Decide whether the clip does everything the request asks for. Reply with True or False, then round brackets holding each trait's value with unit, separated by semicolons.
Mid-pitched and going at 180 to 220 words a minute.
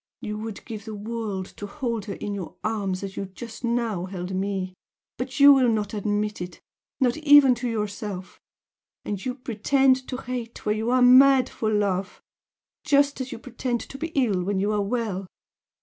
False (220 Hz; 185 wpm)